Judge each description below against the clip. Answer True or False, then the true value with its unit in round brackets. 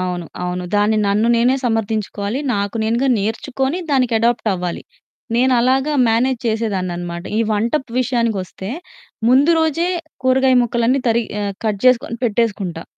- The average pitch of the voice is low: False (230 Hz)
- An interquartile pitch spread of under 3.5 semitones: False (4.1 semitones)